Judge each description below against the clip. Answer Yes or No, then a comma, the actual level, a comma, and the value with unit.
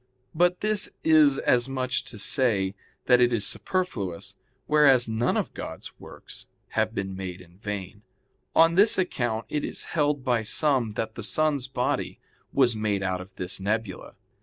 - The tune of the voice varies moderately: No, wide, 6.2 semitones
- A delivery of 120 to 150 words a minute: No, average, 165 wpm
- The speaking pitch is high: No, low, 120 Hz